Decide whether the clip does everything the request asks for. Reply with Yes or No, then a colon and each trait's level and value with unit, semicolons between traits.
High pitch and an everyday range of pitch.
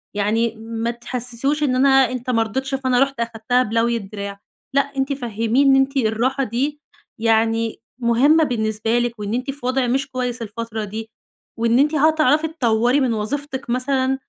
Yes: high, 245 Hz; average, 3.0 semitones